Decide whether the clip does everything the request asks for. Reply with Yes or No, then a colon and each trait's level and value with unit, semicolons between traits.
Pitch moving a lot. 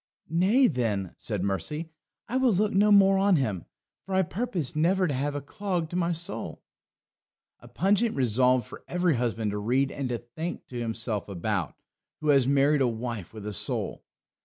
Yes: wide, 8.0 semitones